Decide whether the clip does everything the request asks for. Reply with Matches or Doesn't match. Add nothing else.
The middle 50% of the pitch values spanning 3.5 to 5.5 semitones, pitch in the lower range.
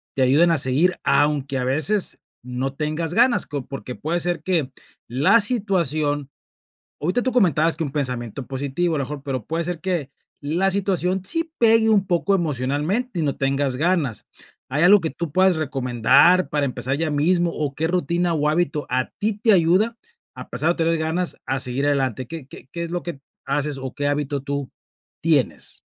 Doesn't match